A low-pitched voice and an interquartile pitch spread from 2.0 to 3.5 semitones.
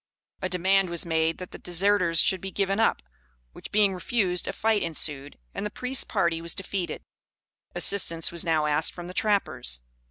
No: medium, 180 Hz; average, 3.2 semitones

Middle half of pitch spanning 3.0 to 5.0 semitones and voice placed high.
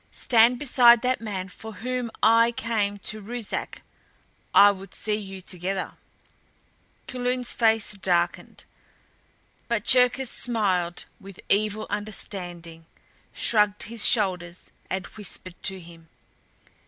Yes: average, 3.8 semitones; high, 210 Hz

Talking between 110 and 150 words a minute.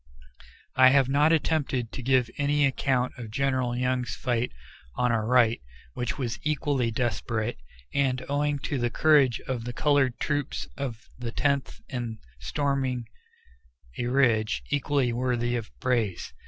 Yes: average, 140 wpm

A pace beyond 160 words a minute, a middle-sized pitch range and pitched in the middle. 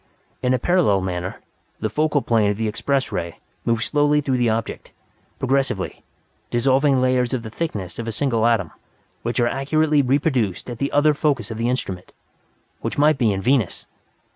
No: average, 175 wpm; average, 4.1 semitones; low, 125 Hz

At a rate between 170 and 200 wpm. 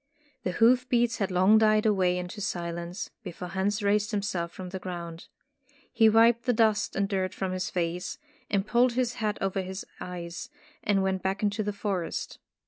Yes: average, 175 wpm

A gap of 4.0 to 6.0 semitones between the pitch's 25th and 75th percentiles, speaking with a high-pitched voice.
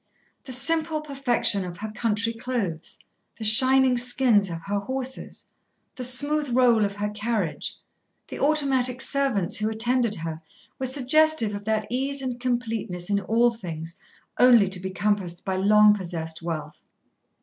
Yes: average, 4.5 semitones; high, 225 Hz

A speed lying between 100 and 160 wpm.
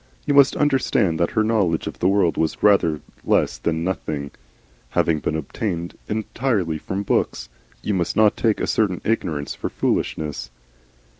Yes: average, 155 wpm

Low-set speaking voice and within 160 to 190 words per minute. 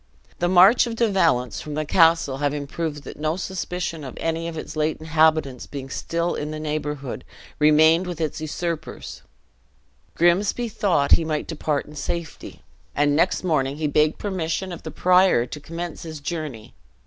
No: medium, 160 Hz; average, 170 wpm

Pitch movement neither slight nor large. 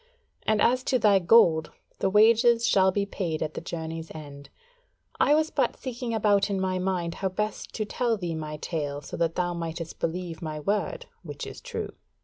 Yes: average, 5.0 semitones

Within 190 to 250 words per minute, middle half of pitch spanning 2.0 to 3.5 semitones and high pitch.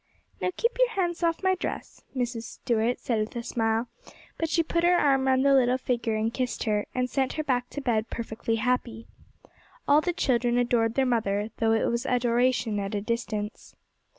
Yes: average, 195 wpm; average, 3.1 semitones; high, 245 Hz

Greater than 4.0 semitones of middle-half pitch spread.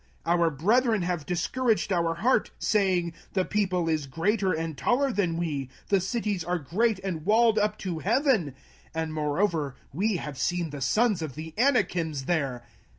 Yes: average, 4.8 semitones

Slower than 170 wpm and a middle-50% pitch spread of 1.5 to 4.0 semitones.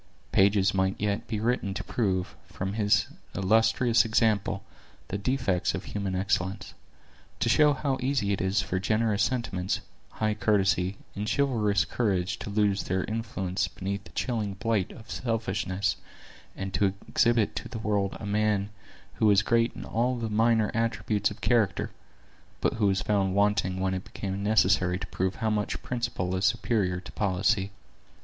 Yes: average, 160 wpm; average, 2.7 semitones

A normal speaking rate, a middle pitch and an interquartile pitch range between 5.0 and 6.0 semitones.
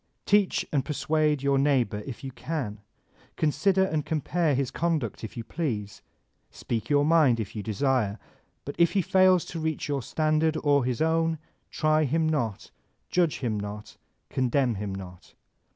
Yes: average, 160 wpm; medium, 145 Hz; wide, 5.6 semitones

